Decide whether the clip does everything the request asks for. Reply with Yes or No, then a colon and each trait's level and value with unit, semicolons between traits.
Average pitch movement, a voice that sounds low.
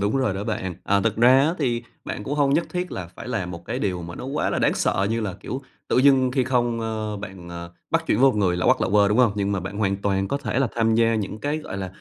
Yes: average, 4.7 semitones; low, 110 Hz